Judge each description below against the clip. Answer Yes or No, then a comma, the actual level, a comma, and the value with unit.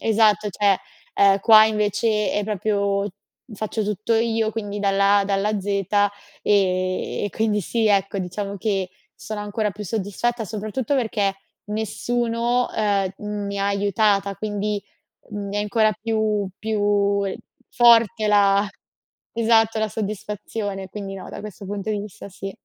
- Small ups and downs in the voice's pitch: Yes, narrow, 1.5 semitones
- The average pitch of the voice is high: Yes, high, 205 Hz